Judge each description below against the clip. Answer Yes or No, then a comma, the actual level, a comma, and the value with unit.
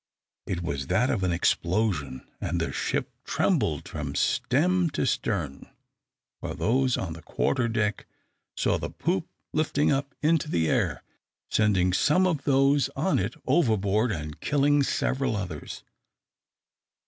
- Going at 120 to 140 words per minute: Yes, slow, 135 wpm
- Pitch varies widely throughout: Yes, wide, 8.2 semitones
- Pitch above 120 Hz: No, low, 115 Hz